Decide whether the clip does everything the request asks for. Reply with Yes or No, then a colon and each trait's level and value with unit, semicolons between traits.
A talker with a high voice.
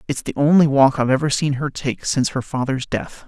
No: medium, 140 Hz